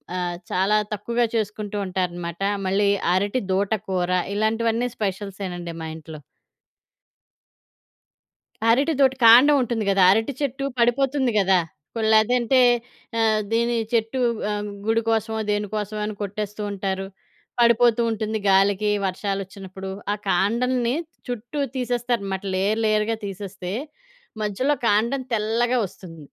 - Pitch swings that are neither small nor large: Yes, average, 3.4 semitones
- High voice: Yes, high, 215 Hz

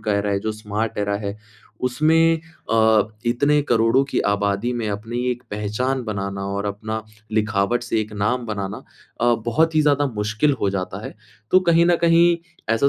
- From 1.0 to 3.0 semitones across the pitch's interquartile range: No, average, 4.3 semitones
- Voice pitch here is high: No, low, 110 Hz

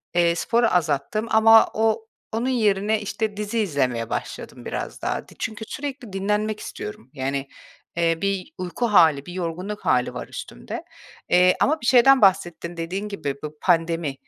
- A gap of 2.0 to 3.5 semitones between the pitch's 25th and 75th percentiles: No, average, 5.0 semitones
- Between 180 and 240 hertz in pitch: Yes, high, 195 Hz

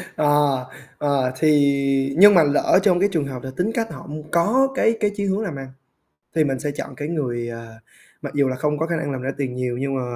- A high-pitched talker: No, medium, 145 Hz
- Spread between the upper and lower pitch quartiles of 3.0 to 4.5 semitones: Yes, average, 4.2 semitones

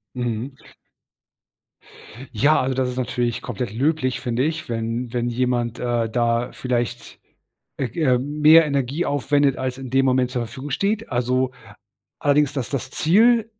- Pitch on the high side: No, low, 130 Hz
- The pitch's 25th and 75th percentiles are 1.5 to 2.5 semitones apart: No, average, 2.9 semitones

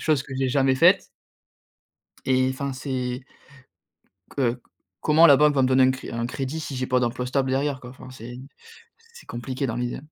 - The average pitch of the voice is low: Yes, low, 130 Hz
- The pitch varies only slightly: Yes, narrow, 1.6 semitones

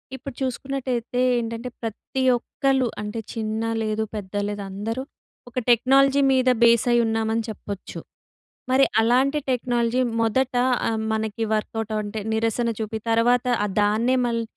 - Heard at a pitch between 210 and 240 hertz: Yes, high, 230 Hz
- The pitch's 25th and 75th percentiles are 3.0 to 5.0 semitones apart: No, narrow, 2.5 semitones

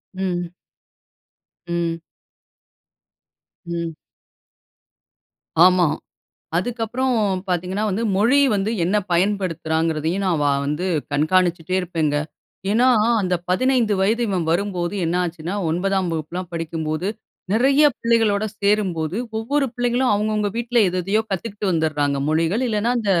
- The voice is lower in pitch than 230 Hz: Yes, medium, 185 Hz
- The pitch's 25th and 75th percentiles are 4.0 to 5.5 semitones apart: Yes, average, 4.3 semitones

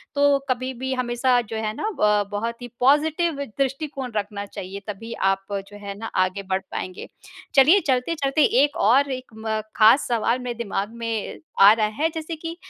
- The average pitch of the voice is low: No, high, 240 Hz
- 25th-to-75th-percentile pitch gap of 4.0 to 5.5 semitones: Yes, average, 4.8 semitones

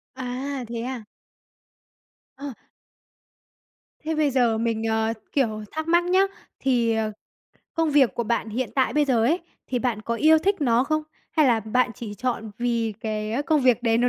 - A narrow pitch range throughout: No, average, 4.0 semitones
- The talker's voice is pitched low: No, high, 245 Hz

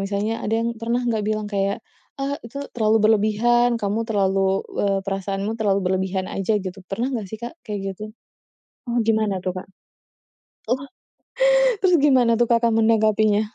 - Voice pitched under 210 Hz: No, high, 215 Hz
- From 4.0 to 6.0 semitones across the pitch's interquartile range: No, average, 2.9 semitones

